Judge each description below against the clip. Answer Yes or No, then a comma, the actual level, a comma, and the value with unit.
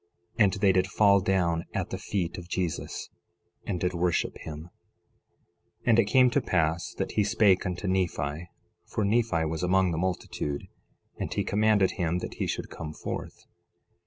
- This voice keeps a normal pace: Yes, average, 170 wpm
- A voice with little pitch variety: No, average, 3.1 semitones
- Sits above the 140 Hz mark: No, very low, 90 Hz